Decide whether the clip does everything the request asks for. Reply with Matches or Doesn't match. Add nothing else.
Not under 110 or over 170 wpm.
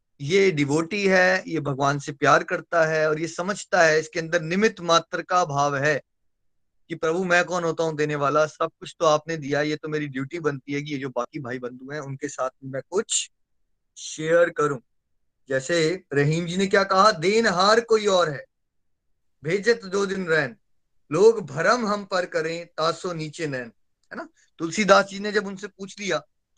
Doesn't match